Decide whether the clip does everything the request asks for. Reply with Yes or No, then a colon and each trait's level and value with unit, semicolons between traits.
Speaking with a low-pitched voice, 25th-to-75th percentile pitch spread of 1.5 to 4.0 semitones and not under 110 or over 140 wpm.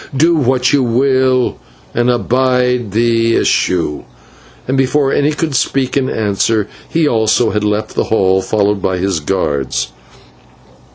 No: low, 120 Hz; average, 4.4 semitones; slow, 135 wpm